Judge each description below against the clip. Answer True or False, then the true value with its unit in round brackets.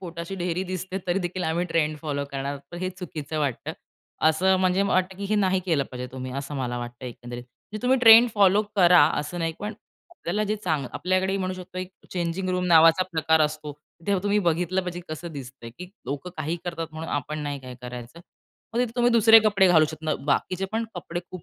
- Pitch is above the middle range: False (175 Hz)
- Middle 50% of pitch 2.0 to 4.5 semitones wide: True (3.9 semitones)